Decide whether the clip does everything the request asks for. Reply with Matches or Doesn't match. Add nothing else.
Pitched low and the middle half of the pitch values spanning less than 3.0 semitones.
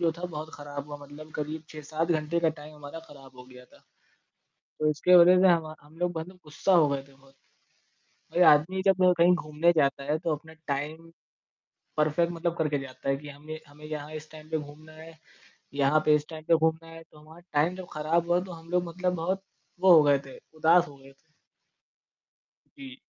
Doesn't match